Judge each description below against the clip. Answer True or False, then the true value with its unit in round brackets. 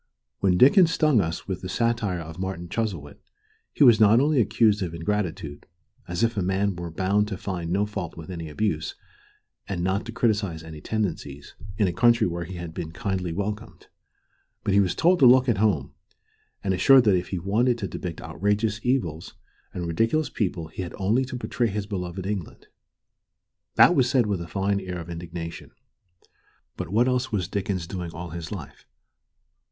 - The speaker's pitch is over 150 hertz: False (95 Hz)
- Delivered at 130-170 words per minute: False (185 wpm)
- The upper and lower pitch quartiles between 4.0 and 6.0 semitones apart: True (4.3 semitones)